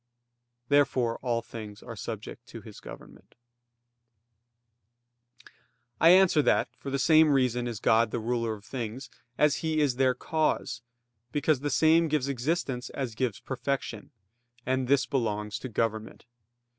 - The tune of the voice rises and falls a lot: No, average, 3.9 semitones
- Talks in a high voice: No, low, 130 Hz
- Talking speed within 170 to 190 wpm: No, average, 140 wpm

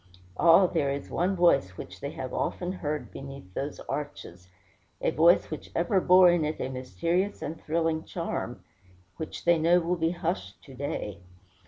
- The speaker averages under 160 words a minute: No, average, 170 wpm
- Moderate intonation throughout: Yes, average, 4.0 semitones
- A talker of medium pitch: Yes, medium, 160 Hz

